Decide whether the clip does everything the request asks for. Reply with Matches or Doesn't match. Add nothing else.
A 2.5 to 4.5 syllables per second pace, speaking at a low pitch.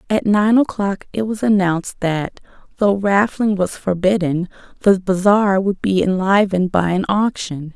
Doesn't match